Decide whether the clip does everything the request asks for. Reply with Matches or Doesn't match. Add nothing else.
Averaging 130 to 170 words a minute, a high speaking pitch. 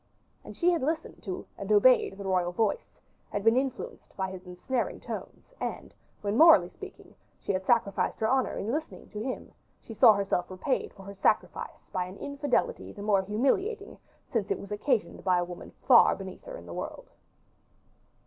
Doesn't match